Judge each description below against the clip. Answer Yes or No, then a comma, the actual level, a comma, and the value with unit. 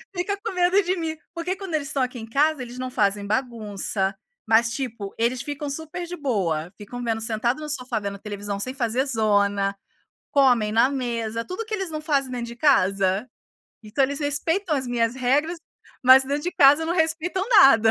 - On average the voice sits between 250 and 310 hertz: Yes, very high, 255 Hz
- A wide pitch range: Yes, wide, 5.7 semitones